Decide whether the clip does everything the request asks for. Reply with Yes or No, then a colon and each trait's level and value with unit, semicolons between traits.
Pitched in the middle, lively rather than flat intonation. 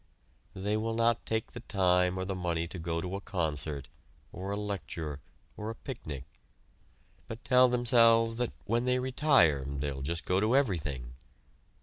No: very low, 95 Hz; wide, 5.8 semitones